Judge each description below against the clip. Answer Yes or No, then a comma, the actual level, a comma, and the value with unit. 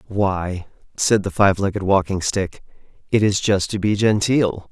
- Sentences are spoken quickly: No, average, 165 wpm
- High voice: No, low, 100 Hz